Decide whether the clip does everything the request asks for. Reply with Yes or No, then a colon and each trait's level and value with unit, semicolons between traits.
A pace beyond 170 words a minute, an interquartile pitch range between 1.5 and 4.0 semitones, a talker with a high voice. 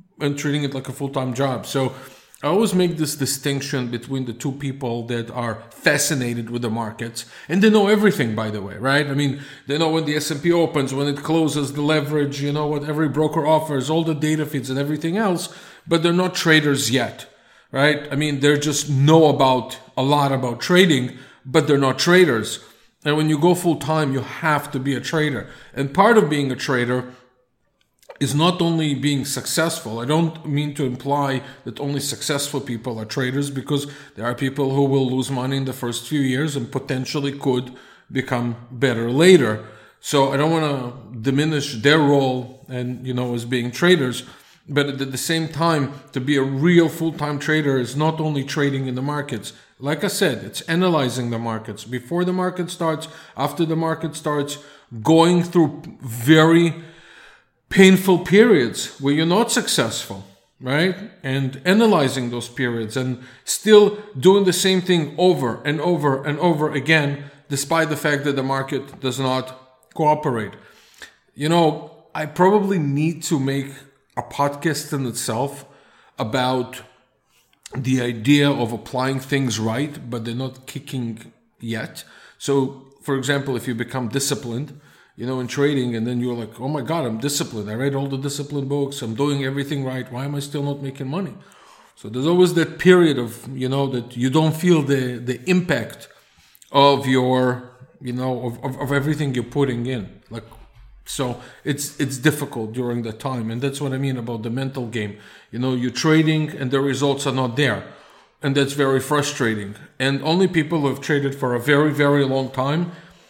No: average, 185 wpm; average, 3.2 semitones; medium, 140 Hz